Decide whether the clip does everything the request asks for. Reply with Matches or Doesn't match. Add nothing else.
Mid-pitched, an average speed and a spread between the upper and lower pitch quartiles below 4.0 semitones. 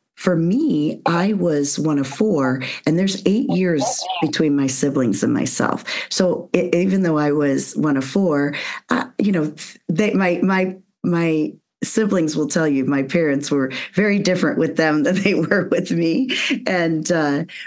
Doesn't match